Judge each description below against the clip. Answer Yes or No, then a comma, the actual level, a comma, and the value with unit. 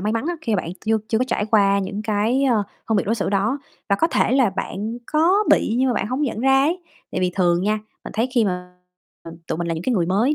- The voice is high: Yes, high, 220 Hz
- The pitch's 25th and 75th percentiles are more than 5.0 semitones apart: No, average, 4.4 semitones